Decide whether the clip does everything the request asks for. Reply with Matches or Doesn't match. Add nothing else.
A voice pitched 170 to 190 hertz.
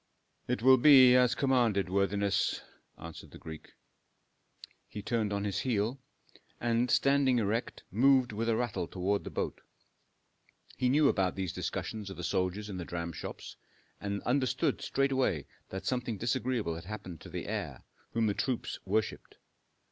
Doesn't match